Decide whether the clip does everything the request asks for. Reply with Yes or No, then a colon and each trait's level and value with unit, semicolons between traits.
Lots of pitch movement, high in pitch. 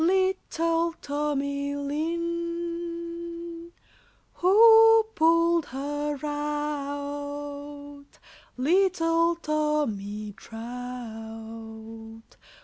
No: average, 3.3 semitones; very high, 295 Hz